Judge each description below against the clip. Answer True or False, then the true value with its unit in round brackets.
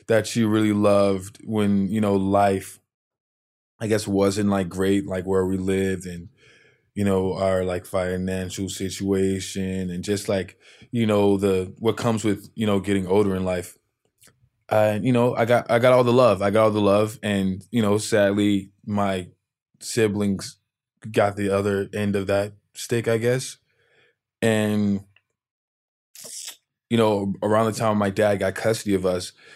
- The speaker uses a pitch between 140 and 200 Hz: False (100 Hz)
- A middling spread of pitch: False (2.3 semitones)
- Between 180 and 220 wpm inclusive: False (165 wpm)